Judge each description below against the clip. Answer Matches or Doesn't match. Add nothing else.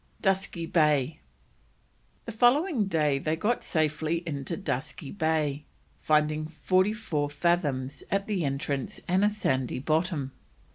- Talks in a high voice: Doesn't match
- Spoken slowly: Matches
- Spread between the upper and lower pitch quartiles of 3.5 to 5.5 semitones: Matches